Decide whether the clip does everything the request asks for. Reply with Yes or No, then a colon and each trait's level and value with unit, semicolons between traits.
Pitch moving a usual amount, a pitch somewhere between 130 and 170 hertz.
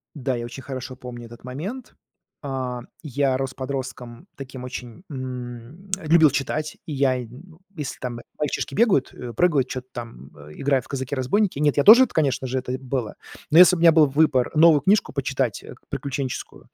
Yes: average, 3.4 semitones; low, 135 Hz